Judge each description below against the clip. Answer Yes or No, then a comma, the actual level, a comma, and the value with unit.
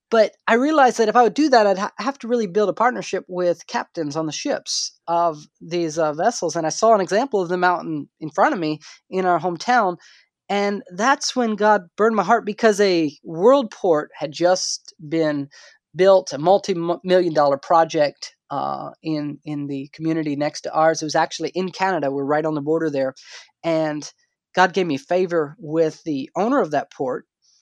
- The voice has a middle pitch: Yes, medium, 180 Hz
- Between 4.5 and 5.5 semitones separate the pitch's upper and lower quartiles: Yes, average, 5.1 semitones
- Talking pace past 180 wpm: Yes, average, 195 wpm